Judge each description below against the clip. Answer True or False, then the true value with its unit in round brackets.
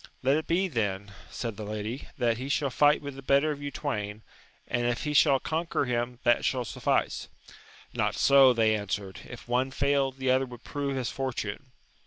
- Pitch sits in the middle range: False (130 Hz)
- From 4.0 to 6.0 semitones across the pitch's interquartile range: False (3.4 semitones)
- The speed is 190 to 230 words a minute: True (195 wpm)